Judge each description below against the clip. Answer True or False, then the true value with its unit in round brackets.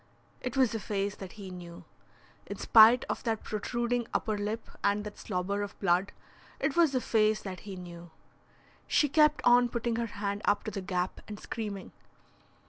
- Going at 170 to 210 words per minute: True (180 wpm)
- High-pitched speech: True (210 Hz)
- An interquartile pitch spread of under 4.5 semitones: True (3.2 semitones)